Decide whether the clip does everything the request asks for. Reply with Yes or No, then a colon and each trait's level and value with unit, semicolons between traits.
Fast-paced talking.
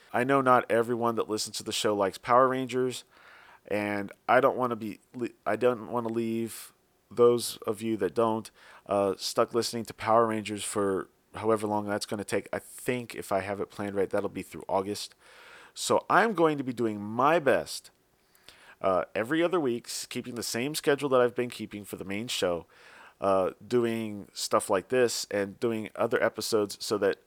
No: average, 195 wpm